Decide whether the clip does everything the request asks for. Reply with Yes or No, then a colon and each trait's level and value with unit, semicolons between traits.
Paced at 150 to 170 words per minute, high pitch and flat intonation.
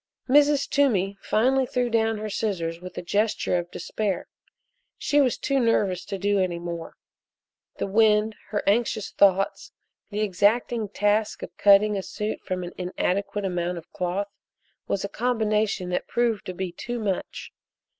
No: average, 155 wpm; high, 205 Hz; average, 3.2 semitones